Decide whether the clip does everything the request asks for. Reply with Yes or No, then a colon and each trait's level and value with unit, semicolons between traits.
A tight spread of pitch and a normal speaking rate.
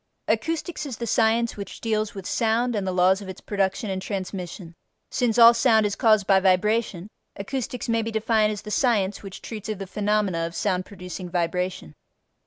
No: average, 3.3 semitones; average, 190 wpm